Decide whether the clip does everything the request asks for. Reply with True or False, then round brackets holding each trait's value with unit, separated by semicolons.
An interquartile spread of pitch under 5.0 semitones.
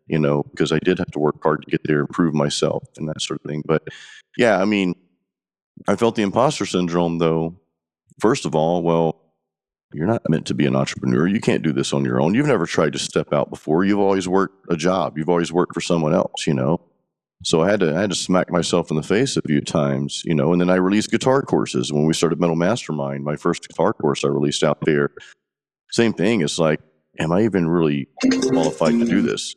True (3.6 semitones)